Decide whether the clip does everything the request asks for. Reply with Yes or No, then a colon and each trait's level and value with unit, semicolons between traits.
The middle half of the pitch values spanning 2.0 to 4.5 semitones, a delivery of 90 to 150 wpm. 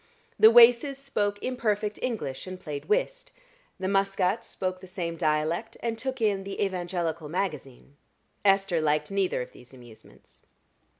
No: average, 5.2 semitones; average, 140 wpm